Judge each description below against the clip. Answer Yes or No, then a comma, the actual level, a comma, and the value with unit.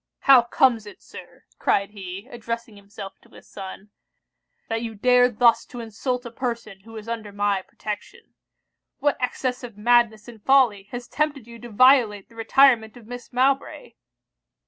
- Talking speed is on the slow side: No, average, 165 wpm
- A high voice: Yes, high, 230 Hz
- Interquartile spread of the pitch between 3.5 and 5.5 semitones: No, average, 3.0 semitones